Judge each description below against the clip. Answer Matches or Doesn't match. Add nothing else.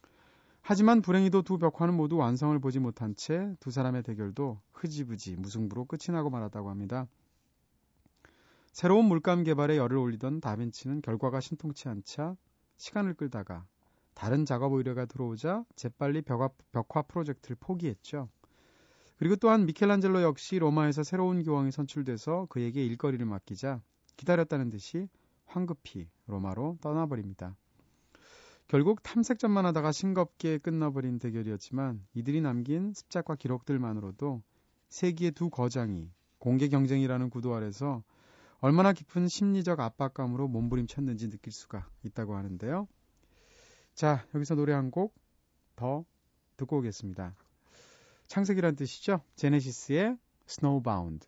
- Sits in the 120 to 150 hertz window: Matches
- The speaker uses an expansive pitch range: Matches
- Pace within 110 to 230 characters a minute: Doesn't match